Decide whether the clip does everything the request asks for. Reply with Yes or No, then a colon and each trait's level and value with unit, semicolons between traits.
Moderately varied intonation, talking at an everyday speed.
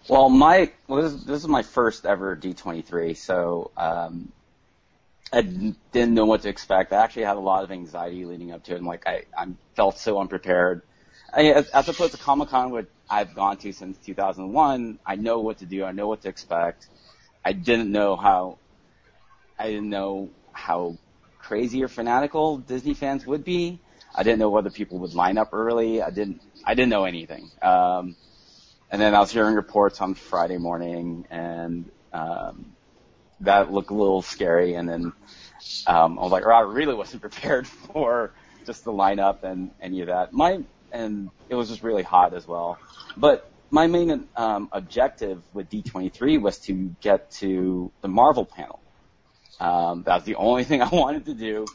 Yes: average, 4.2 semitones; average, 185 wpm